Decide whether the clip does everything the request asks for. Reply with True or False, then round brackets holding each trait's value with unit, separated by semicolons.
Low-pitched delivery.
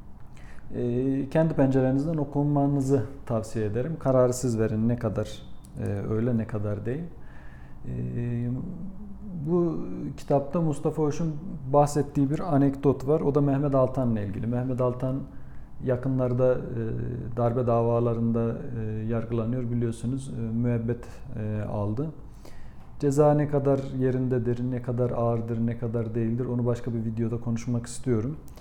True (125 Hz)